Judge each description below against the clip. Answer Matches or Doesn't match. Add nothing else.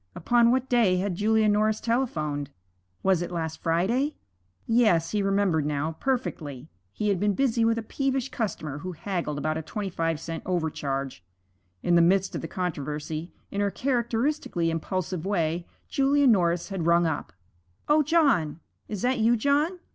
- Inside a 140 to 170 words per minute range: Matches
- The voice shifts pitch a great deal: Matches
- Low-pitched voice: Doesn't match